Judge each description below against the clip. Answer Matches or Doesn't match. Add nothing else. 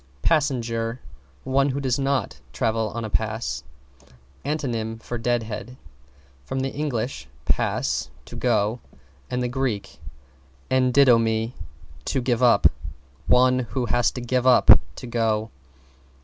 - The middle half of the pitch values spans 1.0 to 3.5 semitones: Matches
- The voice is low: Matches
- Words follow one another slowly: Matches